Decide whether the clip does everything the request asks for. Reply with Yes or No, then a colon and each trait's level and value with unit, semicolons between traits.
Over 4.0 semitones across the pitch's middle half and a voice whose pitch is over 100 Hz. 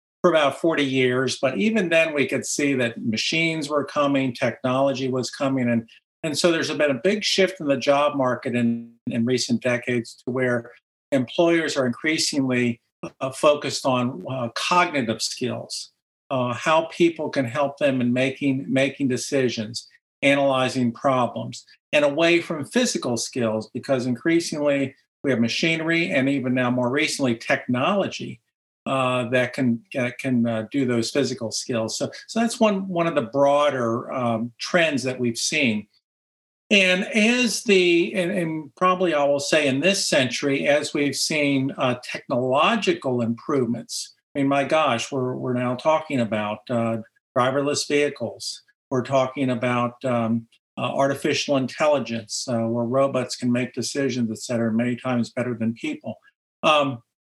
No: average, 3.7 semitones; low, 135 Hz